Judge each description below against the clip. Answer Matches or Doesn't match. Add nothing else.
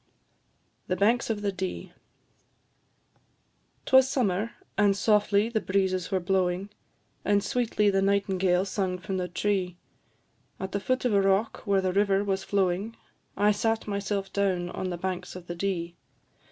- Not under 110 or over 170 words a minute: Matches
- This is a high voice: Matches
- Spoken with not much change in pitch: Matches